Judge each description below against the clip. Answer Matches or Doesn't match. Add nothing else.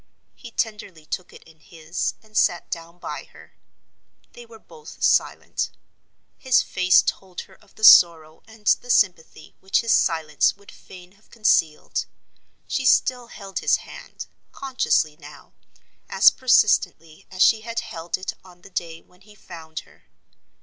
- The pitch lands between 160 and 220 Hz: Matches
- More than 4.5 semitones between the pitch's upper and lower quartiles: Matches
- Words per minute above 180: Doesn't match